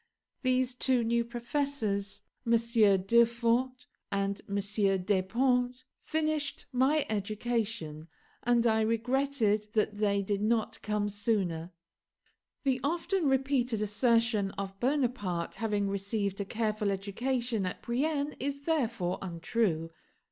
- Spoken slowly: Yes, slow, 105 wpm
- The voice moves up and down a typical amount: Yes, average, 4.0 semitones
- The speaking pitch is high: Yes, high, 225 Hz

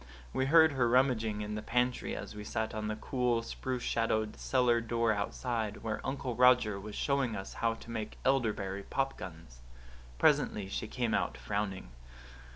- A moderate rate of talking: Yes, average, 165 wpm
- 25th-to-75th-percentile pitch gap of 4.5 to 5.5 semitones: No, average, 3.0 semitones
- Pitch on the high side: No, low, 115 Hz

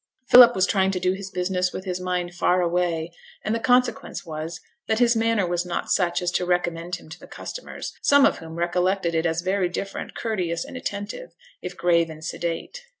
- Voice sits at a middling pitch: Yes, medium, 180 Hz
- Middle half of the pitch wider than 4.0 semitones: No, average, 2.8 semitones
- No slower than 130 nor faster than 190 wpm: No, fast, 205 wpm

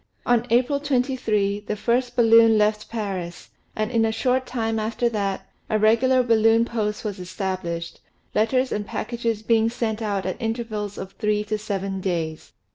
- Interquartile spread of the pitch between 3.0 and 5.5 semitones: No, narrow, 2.4 semitones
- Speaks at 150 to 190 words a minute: Yes, average, 160 wpm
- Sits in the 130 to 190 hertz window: No, high, 220 Hz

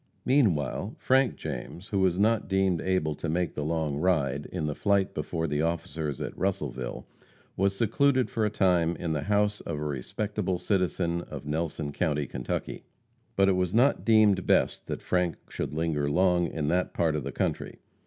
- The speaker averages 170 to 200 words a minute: Yes, average, 180 wpm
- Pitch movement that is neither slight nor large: Yes, average, 4.4 semitones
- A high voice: No, very low, 85 Hz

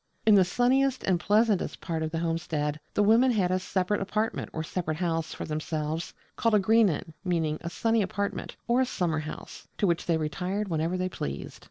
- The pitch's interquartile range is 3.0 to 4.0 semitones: No, average, 4.5 semitones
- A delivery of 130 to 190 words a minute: No, average, 200 wpm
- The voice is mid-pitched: Yes, medium, 180 Hz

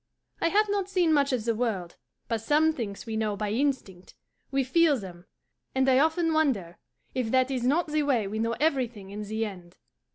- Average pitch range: No, wide, 6.0 semitones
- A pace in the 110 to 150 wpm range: No, average, 200 wpm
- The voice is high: Yes, very high, 250 Hz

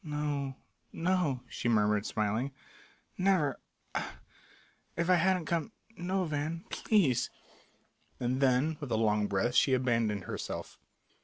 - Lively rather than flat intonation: Yes, wide, 6.1 semitones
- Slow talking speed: Yes, slow, 130 wpm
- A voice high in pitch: No, medium, 140 Hz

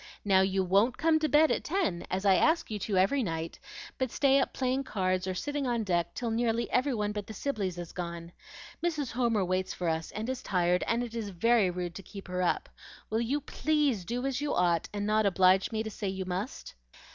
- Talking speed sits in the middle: No, fast, 230 wpm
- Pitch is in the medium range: No, high, 210 Hz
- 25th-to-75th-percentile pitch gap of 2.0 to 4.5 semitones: No, wide, 5.4 semitones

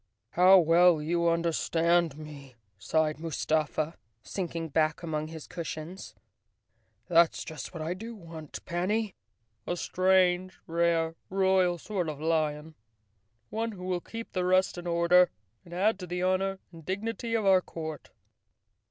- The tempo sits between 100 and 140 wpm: Yes, slow, 135 wpm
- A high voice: No, medium, 170 Hz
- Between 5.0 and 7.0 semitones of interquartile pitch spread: No, average, 2.7 semitones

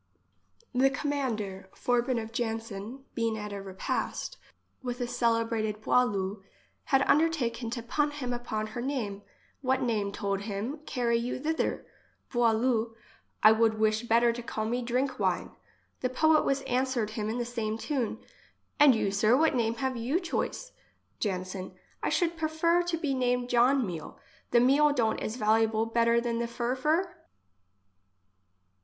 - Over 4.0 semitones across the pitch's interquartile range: No, average, 3.3 semitones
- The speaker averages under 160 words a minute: No, average, 165 wpm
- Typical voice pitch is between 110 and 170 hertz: No, high, 235 Hz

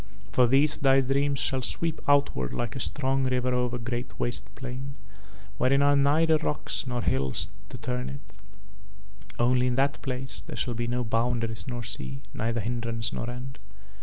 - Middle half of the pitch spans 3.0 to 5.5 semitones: No, narrow, 2.5 semitones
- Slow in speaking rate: No, average, 170 wpm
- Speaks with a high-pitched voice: No, low, 125 Hz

